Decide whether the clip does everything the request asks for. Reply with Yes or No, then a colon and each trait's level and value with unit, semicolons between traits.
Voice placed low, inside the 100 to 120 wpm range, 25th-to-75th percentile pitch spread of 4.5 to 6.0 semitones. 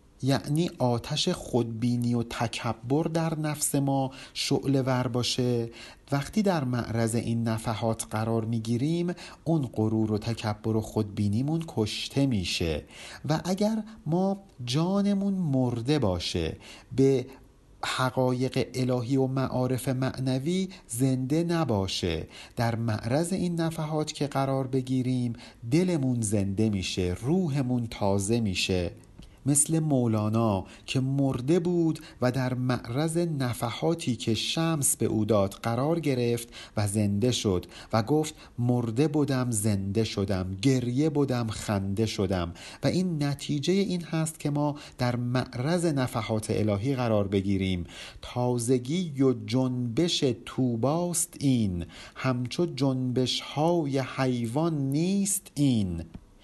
Yes: low, 125 Hz; average, 110 wpm; average, 4.8 semitones